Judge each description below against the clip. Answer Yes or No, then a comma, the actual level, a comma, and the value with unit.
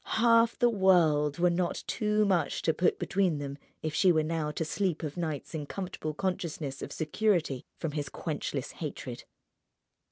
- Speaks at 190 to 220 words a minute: No, average, 165 wpm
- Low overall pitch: No, medium, 165 Hz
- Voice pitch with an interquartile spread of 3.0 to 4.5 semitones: Yes, average, 4.0 semitones